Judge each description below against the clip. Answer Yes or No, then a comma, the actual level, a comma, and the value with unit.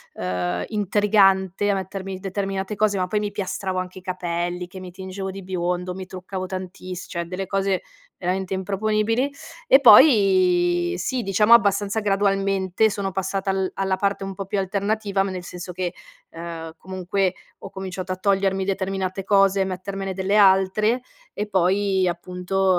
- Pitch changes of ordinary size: No, narrow, 1.3 semitones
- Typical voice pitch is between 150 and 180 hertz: No, high, 190 Hz